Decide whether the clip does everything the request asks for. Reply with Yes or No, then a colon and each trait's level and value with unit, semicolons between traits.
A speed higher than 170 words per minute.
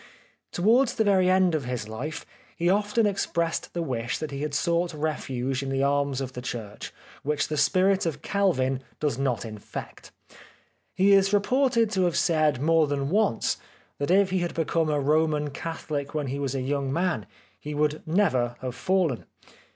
Yes: average, 180 wpm